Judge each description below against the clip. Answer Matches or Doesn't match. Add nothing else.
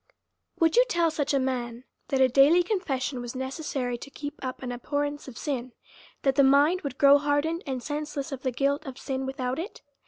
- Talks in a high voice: Matches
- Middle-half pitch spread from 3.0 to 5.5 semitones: Doesn't match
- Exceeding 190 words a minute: Matches